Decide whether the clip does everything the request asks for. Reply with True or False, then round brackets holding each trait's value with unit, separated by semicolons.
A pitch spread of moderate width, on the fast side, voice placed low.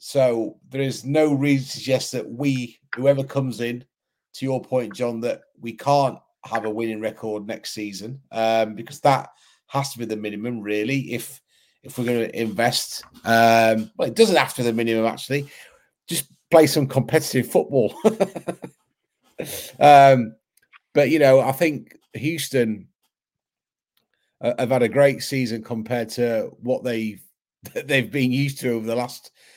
False (3.1 semitones; 160 wpm; 125 Hz)